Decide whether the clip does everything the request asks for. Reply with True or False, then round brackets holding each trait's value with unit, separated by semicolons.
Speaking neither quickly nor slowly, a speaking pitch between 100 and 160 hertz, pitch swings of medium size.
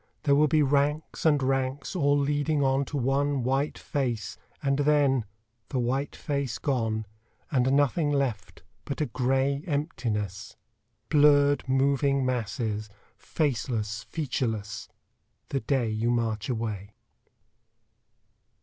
False (115 wpm; 135 Hz; 3.7 semitones)